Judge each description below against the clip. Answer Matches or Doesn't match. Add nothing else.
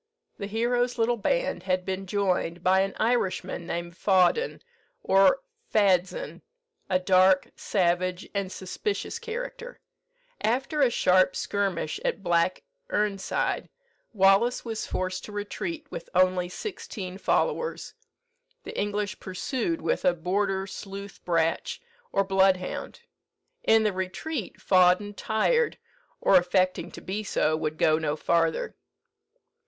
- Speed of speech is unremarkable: Doesn't match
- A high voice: Matches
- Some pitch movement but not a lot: Matches